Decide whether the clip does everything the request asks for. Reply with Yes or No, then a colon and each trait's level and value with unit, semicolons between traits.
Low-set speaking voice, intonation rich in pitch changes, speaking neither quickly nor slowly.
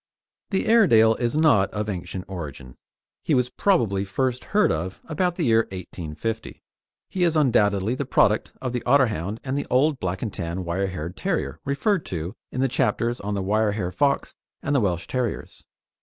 Yes: low, 110 Hz; wide, 6.7 semitones; average, 180 wpm